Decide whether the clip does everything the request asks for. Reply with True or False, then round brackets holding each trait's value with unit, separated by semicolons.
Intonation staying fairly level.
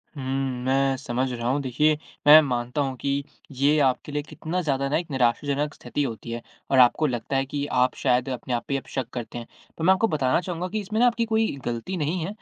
False (3.6 semitones)